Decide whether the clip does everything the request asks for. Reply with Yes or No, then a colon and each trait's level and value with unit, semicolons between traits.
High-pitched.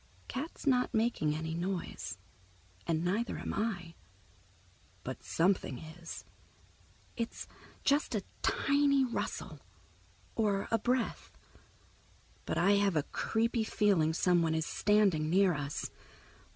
Yes: high, 195 Hz